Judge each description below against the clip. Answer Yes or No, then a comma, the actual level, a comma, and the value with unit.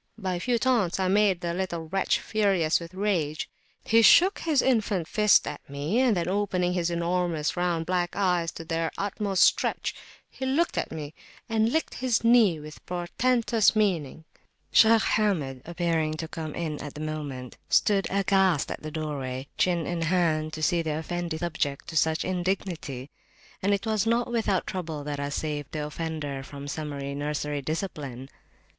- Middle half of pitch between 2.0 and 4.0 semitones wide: No, average, 4.5 semitones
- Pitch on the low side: No, medium, 175 Hz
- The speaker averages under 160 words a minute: No, average, 170 wpm